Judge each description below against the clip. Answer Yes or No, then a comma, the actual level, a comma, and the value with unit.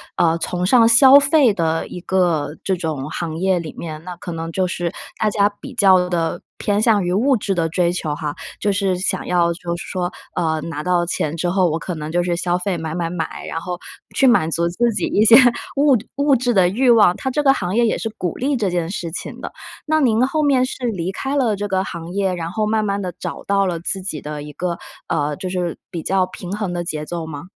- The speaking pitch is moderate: Yes, medium, 180 Hz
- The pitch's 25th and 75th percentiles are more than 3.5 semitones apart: Yes, average, 4.2 semitones